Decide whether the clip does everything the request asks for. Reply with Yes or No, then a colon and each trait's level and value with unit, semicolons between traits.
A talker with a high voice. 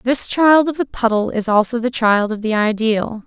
Yes: high, 230 Hz